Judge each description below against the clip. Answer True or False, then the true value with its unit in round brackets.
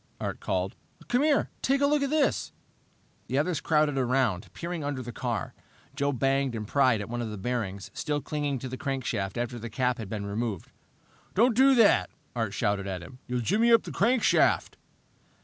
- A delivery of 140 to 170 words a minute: False (185 wpm)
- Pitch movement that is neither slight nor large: False (6.2 semitones)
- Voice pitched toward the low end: True (130 Hz)